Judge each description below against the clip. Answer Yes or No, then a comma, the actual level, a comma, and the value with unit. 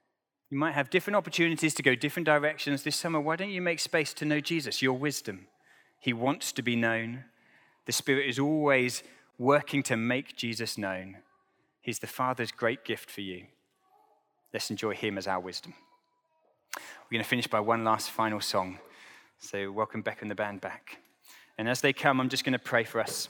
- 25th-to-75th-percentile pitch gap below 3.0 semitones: No, average, 4.9 semitones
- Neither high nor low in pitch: No, low, 130 Hz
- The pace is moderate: Yes, average, 195 wpm